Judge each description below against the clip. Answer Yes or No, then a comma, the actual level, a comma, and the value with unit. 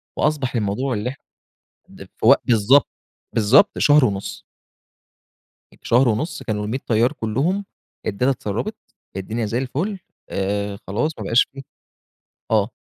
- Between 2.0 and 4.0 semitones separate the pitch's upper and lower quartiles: No, average, 4.7 semitones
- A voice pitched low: Yes, low, 120 Hz